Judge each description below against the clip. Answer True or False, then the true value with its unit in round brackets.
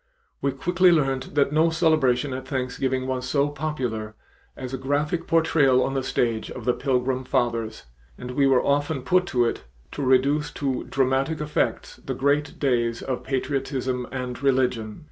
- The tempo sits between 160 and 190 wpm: True (165 wpm)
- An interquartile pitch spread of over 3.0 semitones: False (2.4 semitones)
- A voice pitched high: False (135 Hz)